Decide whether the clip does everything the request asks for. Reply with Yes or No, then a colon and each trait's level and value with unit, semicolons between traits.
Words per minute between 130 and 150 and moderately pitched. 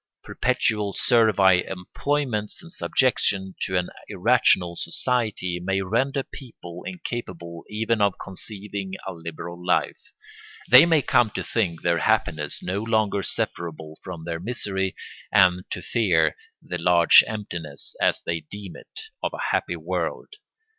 No: slow, 135 wpm; very low, 95 Hz